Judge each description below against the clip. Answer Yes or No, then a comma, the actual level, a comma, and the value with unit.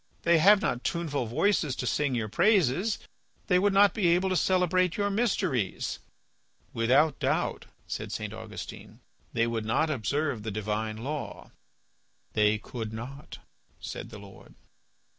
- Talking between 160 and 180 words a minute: No, average, 140 wpm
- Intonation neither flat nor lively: No, wide, 8.3 semitones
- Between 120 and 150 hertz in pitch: Yes, medium, 140 Hz